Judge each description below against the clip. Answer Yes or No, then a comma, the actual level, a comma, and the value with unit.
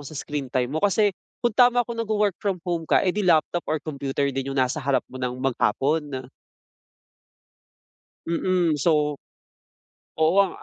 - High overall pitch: No, medium, 155 Hz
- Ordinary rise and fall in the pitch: No, wide, 5.8 semitones